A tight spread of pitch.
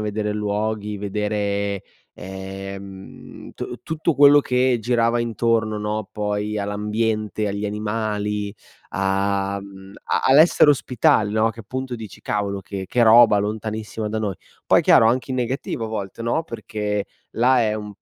Yes: narrow, 2.2 semitones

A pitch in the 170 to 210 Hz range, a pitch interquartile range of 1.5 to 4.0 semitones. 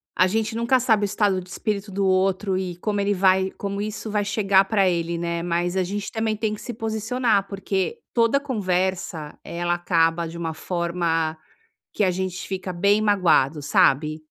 Yes: high, 190 Hz; average, 3.3 semitones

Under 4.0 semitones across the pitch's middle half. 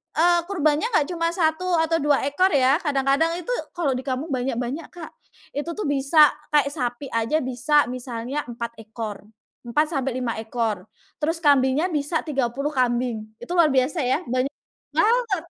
No: average, 4.3 semitones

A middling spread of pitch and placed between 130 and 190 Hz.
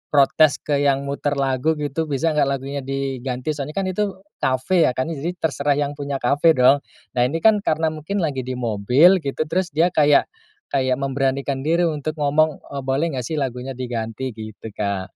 Yes: average, 3.1 semitones; medium, 140 Hz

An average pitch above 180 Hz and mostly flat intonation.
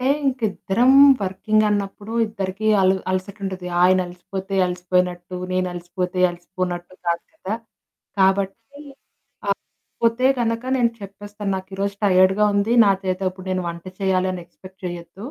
Yes: high, 190 Hz; narrow, 2.0 semitones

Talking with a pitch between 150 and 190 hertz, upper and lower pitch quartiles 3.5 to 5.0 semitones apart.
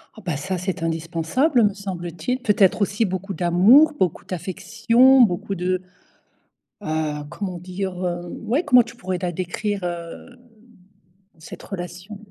Yes: medium, 185 Hz; average, 3.8 semitones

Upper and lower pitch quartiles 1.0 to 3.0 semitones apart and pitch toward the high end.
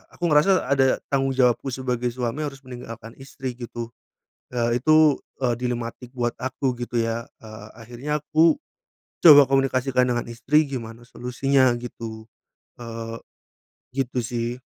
No: narrow, 2.5 semitones; low, 125 Hz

